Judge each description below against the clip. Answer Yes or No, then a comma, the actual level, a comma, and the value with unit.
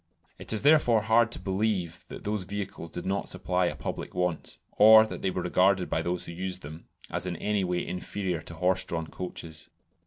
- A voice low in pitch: Yes, very low, 90 Hz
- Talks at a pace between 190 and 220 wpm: Yes, fast, 205 wpm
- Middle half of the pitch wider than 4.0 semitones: No, average, 2.7 semitones